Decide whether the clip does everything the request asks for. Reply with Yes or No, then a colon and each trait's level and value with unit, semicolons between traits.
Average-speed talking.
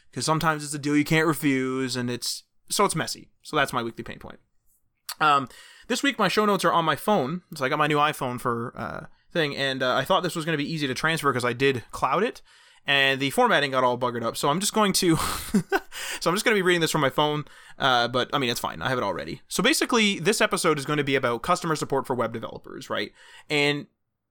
No: fast, 255 wpm